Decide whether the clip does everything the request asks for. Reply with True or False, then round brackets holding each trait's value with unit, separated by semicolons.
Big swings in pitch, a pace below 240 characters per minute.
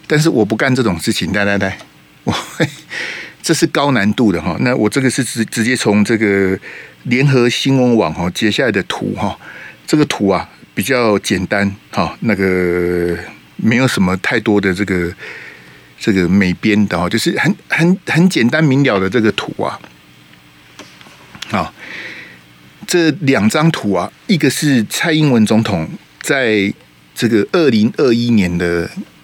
True (6.3 semitones; 220 characters per minute)